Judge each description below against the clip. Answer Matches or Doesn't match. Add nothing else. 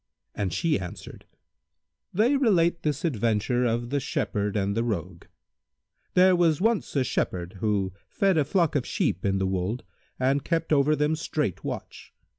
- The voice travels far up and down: Matches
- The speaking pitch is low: Matches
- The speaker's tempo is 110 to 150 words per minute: Doesn't match